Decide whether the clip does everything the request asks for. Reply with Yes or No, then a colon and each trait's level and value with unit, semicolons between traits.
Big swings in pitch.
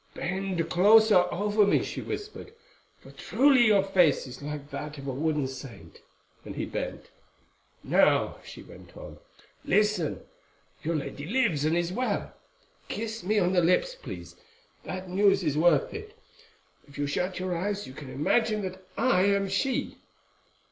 Yes: wide, 5.7 semitones